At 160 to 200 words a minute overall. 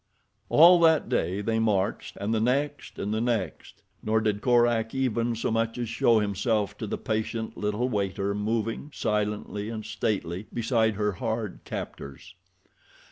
No: average, 150 wpm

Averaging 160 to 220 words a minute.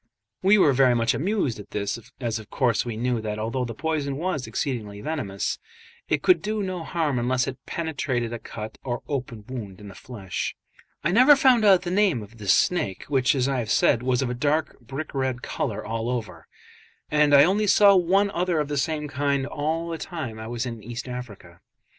Yes: fast, 205 wpm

